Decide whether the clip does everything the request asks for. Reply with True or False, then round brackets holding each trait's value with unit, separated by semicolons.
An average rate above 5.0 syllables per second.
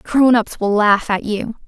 False (4.1 syllables/s)